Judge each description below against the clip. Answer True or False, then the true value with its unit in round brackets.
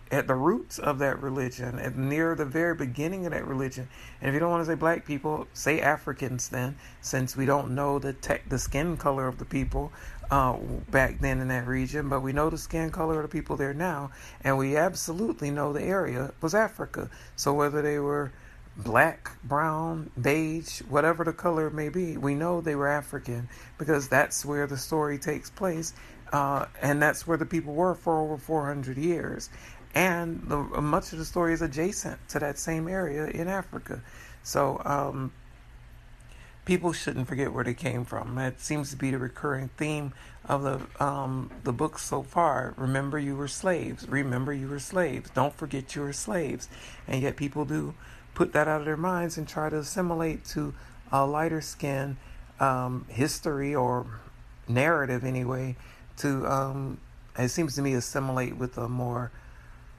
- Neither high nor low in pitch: True (145 Hz)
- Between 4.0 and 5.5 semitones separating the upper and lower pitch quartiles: False (3.1 semitones)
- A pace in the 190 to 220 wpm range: False (180 wpm)